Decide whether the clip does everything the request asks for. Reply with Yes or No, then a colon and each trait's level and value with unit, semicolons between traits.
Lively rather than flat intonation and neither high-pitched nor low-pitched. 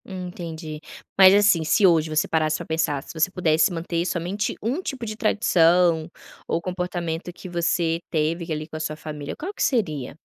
No: average, 2.8 semitones; medium, 170 Hz